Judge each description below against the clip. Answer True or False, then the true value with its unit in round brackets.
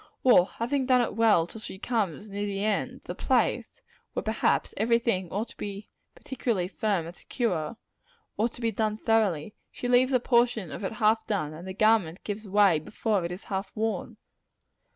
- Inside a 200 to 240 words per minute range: False (190 wpm)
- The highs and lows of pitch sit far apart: False (3.2 semitones)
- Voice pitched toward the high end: True (215 Hz)